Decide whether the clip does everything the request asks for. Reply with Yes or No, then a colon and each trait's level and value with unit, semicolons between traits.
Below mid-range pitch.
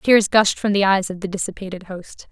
No: high, 195 Hz